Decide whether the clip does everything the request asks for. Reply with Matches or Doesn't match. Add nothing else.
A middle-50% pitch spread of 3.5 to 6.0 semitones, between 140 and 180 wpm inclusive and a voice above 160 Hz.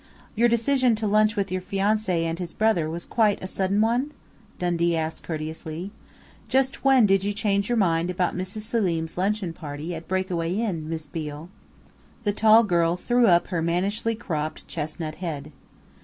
Matches